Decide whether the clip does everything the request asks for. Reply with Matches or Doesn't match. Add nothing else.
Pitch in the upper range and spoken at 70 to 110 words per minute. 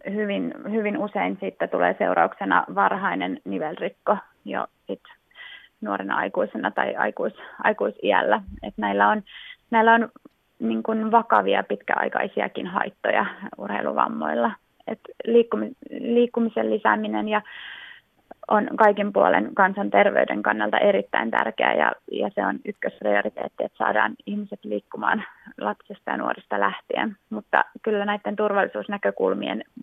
Matches